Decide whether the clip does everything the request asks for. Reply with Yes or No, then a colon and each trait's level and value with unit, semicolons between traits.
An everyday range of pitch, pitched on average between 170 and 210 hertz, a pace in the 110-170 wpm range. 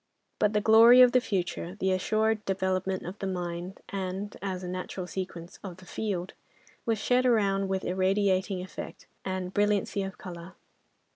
No: narrow, 2.0 semitones; high, 190 Hz; average, 160 wpm